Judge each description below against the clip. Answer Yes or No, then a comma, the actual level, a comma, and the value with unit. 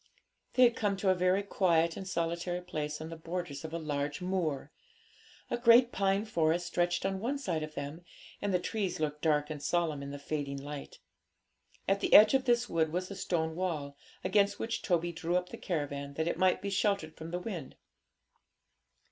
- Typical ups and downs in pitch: Yes, average, 3.9 semitones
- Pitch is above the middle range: No, medium, 175 Hz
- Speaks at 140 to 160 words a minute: No, average, 200 wpm